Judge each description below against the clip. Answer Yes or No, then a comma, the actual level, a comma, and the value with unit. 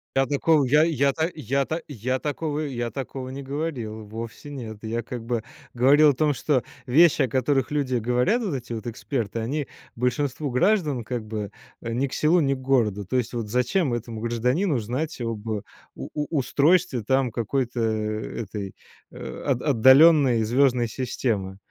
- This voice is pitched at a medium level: No, low, 130 Hz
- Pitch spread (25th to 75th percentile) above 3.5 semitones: Yes, average, 3.9 semitones